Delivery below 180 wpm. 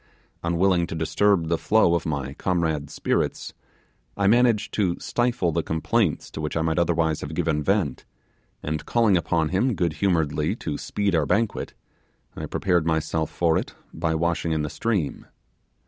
Yes: average, 165 wpm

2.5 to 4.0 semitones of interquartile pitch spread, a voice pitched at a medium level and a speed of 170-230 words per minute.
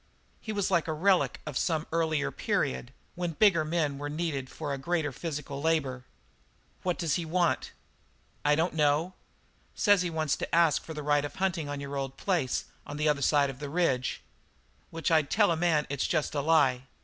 Yes: average, 2.9 semitones; medium, 155 Hz; average, 195 wpm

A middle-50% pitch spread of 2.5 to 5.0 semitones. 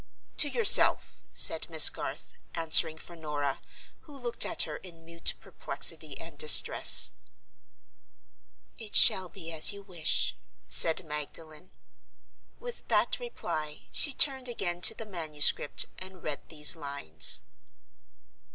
No: wide, 5.4 semitones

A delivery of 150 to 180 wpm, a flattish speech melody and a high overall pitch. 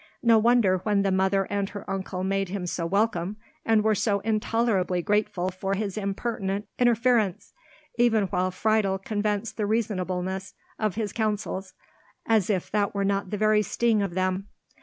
Yes: average, 160 wpm; narrow, 2.3 semitones; high, 200 Hz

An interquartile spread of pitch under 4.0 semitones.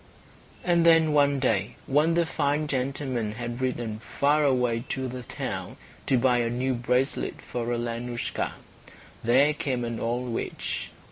Yes: average, 3.2 semitones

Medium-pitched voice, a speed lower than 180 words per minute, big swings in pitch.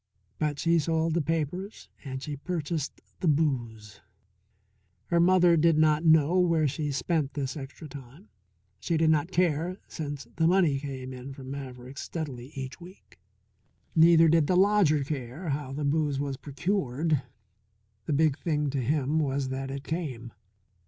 No: medium, 150 Hz; average, 155 wpm; average, 3.3 semitones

